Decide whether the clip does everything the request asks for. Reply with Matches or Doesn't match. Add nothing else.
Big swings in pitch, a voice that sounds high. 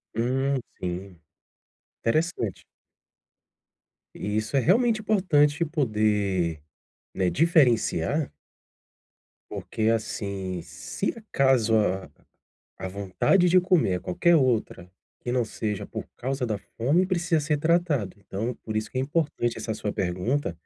Doesn't match